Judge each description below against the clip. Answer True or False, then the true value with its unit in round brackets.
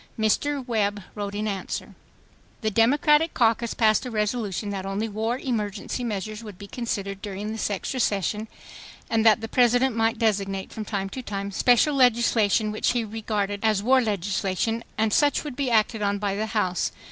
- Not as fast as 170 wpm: False (175 wpm)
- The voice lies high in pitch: True (215 Hz)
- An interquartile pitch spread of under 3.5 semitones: True (2.6 semitones)